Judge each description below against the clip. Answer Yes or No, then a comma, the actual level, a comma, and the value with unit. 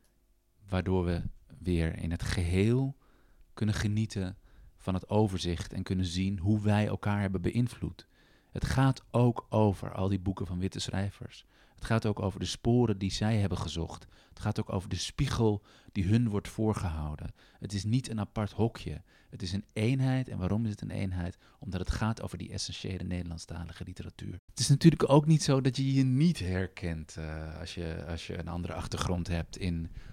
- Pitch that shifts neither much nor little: Yes, average, 3.9 semitones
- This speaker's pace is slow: No, average, 185 wpm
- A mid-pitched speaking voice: No, low, 100 Hz